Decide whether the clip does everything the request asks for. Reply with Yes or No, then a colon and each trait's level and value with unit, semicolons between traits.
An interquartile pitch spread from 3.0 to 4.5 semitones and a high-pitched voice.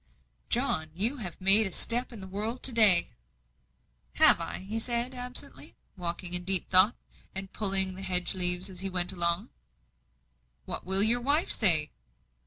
Yes: average, 4.0 semitones; high, 195 Hz